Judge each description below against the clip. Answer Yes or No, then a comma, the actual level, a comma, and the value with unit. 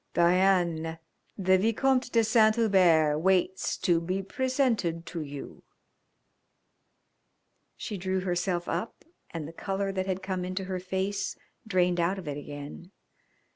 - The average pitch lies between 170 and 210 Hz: Yes, medium, 185 Hz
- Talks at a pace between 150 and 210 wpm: No, slow, 135 wpm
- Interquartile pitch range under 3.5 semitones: Yes, narrow, 2.5 semitones